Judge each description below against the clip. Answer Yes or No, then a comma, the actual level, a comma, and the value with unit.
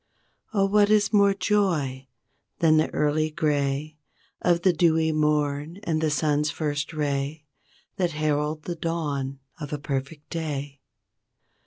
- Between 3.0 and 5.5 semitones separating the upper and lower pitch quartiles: No, narrow, 2.5 semitones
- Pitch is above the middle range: No, medium, 155 Hz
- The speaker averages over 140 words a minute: No, slow, 135 wpm